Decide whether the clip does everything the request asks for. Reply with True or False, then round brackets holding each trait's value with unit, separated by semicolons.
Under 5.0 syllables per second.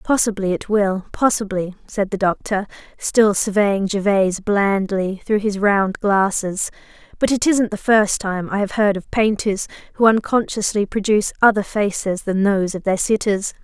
True (4.6 syllables/s)